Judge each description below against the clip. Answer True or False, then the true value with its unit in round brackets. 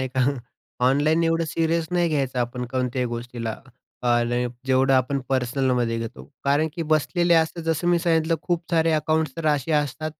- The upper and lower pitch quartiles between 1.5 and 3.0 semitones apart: False (4.3 semitones)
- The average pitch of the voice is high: False (145 Hz)